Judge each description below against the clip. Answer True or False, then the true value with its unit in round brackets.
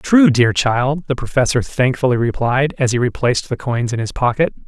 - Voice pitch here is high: False (130 Hz)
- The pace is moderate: True (190 wpm)